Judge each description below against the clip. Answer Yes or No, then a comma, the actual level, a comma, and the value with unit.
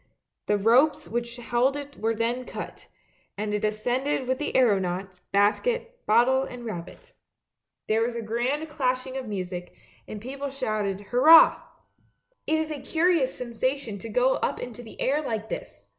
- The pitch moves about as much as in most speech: Yes, average, 4.3 semitones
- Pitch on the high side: Yes, high, 245 Hz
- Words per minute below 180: Yes, average, 170 wpm